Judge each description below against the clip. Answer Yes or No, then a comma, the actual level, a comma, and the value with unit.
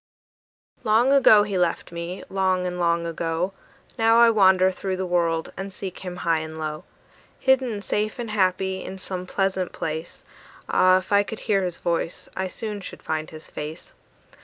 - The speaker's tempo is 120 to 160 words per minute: No, average, 175 wpm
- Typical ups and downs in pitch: Yes, average, 3.1 semitones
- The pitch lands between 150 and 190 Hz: Yes, medium, 185 Hz